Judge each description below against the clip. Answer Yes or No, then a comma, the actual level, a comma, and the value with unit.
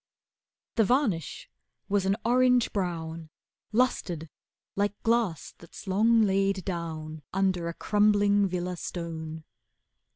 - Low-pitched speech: No, high, 190 Hz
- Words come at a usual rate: No, slow, 105 wpm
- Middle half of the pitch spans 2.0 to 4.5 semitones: Yes, average, 3.8 semitones